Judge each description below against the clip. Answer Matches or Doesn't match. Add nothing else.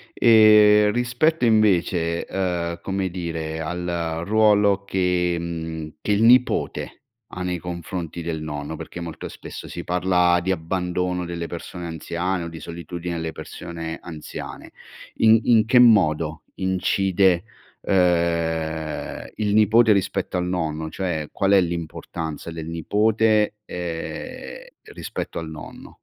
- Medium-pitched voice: Doesn't match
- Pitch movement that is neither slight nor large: Matches